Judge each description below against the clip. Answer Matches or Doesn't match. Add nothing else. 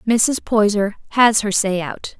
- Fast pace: Doesn't match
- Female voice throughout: Matches